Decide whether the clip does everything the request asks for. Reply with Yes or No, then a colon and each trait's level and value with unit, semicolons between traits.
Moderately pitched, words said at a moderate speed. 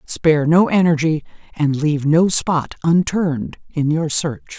Yes: medium, 160 Hz; average, 145 wpm